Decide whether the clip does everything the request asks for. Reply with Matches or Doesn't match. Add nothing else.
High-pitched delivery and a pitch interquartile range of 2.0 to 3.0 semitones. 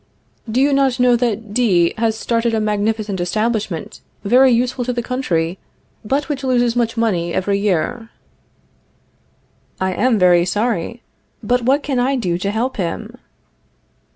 Doesn't match